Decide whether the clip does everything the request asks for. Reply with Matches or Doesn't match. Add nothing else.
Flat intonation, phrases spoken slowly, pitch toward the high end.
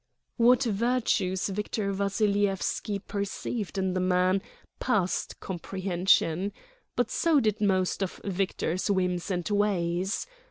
Matches